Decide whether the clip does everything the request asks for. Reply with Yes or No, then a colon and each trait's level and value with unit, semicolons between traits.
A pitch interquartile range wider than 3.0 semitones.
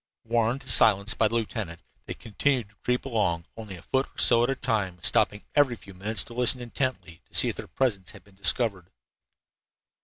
Yes: average, 3.9 semitones